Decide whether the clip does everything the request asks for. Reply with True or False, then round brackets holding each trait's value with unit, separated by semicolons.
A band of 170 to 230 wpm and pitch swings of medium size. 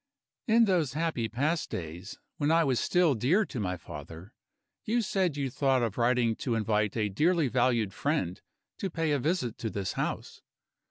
False (175 wpm; 7.2 semitones)